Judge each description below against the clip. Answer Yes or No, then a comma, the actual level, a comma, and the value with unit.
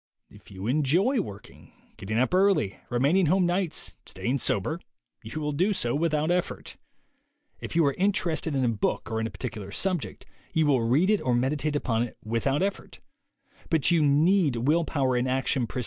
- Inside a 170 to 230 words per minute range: No, average, 150 wpm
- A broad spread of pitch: Yes, wide, 6.9 semitones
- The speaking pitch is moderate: Yes, medium, 145 Hz